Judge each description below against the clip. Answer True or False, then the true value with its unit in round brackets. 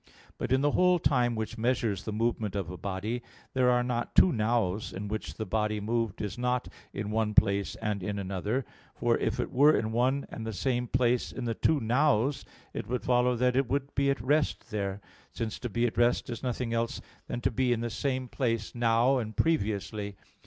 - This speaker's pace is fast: True (210 wpm)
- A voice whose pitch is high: False (120 Hz)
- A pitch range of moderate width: True (3.0 semitones)